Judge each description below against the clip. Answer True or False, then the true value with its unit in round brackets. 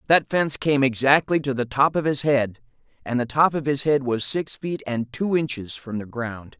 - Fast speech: True (230 wpm)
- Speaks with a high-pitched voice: False (135 Hz)